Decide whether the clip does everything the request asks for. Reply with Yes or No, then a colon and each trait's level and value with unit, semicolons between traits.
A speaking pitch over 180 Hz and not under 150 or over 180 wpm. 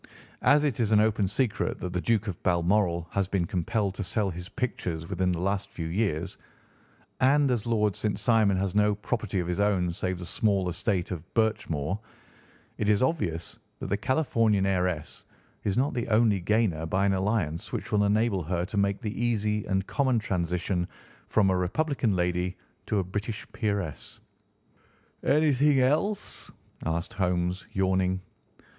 No: low, 100 Hz; average, 165 wpm